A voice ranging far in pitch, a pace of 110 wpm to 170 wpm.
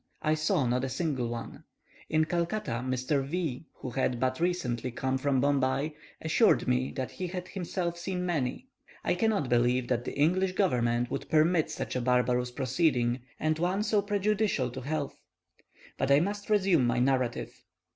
Yes: wide, 5.9 semitones; average, 165 wpm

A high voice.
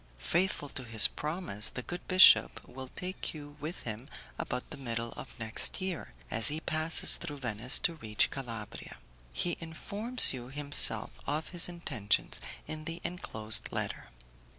No: medium, 145 Hz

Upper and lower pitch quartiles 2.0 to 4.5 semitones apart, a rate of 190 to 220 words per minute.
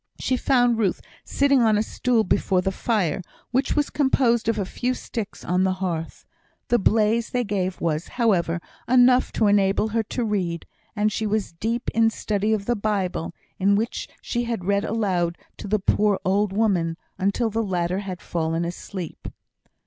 No: average, 3.6 semitones; average, 175 wpm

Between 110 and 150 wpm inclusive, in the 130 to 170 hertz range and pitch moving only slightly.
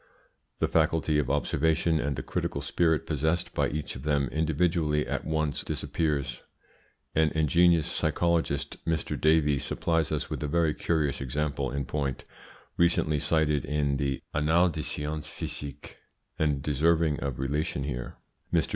No: average, 145 wpm; very low, 75 Hz; narrow, 2.2 semitones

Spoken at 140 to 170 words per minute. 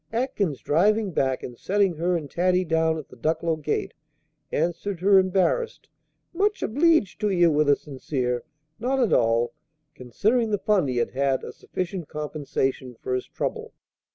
Yes: average, 160 wpm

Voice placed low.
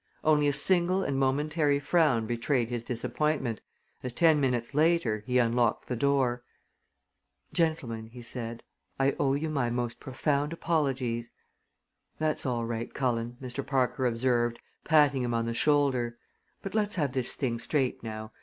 Yes: low, 130 Hz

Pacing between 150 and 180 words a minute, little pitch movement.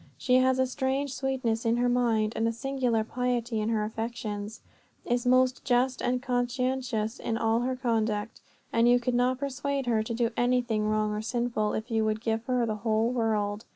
No: average, 190 wpm; narrow, 2.2 semitones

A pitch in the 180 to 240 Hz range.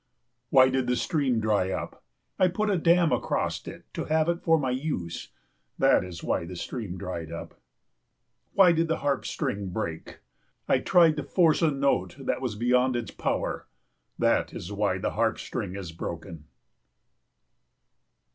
No: low, 125 Hz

